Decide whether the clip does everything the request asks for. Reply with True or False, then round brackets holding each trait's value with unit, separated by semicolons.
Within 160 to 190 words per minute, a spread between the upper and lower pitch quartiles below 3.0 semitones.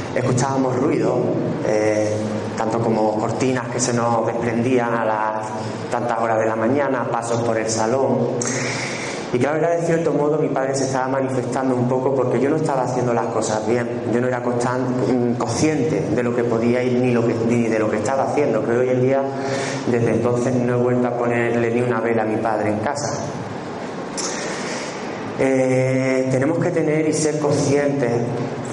True (185 wpm; 2.5 semitones)